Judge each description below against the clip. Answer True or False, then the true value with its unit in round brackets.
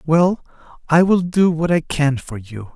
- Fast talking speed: False (195 wpm)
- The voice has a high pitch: False (155 Hz)